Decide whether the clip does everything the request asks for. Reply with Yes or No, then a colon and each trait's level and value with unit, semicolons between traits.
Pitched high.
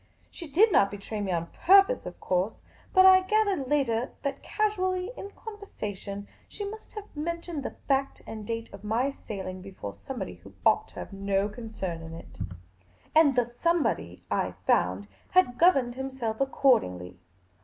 Yes: very high, 250 Hz